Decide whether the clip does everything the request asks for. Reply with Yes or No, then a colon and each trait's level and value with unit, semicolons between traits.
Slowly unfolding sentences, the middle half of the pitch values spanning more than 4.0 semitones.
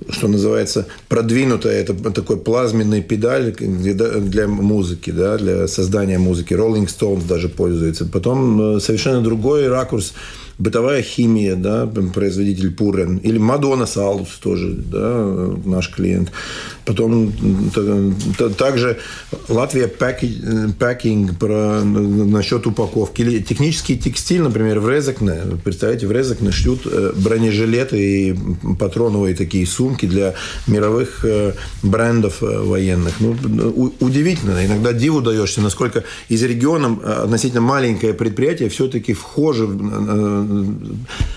No: slow, 105 wpm; average, 3.2 semitones